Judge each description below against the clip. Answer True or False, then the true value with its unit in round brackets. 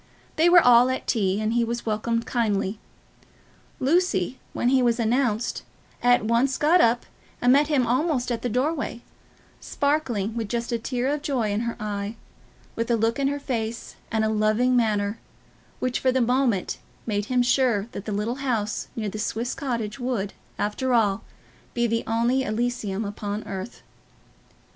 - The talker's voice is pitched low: False (235 Hz)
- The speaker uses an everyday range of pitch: True (3.0 semitones)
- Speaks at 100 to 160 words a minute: False (170 wpm)